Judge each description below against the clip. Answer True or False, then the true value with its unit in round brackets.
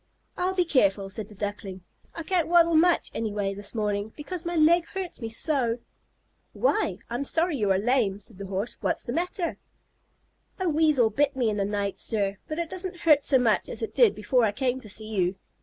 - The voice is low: False (245 Hz)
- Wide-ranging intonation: True (8.3 semitones)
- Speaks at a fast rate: True (210 wpm)